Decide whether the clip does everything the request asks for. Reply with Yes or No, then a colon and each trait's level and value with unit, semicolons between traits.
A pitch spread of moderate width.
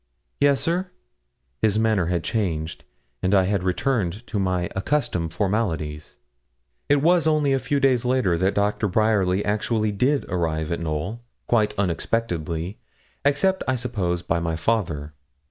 No: wide, 6.1 semitones